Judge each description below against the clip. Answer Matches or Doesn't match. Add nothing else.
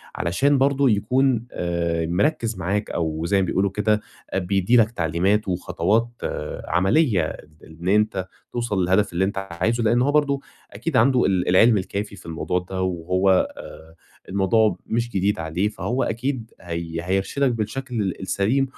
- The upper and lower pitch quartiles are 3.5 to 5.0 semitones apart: Matches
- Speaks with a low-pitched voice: Matches